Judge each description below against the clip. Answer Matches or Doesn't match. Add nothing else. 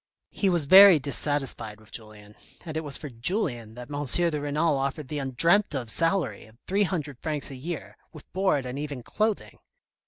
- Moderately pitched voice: Matches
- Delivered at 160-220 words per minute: Matches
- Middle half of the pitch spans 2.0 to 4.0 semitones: Doesn't match